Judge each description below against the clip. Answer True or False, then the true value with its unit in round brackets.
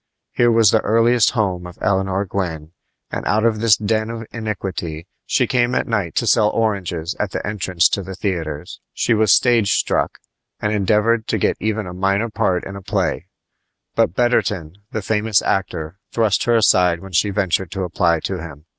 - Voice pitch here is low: True (100 Hz)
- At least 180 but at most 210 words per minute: True (185 wpm)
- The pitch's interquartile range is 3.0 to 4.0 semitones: True (3.5 semitones)